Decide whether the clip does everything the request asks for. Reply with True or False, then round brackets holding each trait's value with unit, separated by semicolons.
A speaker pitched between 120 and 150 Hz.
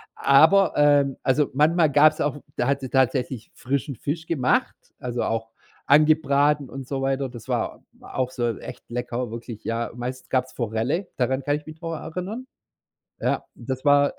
True (135 Hz)